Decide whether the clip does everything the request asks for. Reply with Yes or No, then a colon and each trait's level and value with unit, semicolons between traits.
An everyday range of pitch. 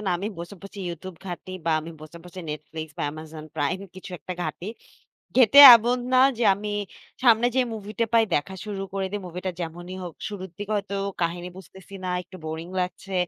Yes: average, 3.4 semitones